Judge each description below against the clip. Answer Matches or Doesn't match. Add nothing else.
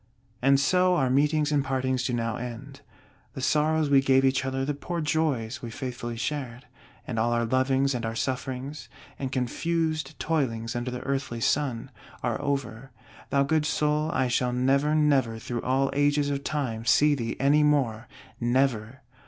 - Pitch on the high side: Doesn't match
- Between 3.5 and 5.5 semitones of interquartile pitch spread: Doesn't match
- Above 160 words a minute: Matches